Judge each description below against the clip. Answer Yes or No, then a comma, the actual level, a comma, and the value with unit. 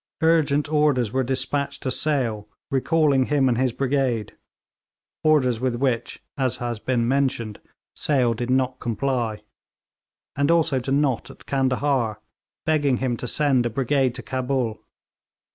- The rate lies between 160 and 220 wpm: No, average, 140 wpm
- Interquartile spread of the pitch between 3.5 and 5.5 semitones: No, narrow, 2.6 semitones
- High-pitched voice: No, low, 130 Hz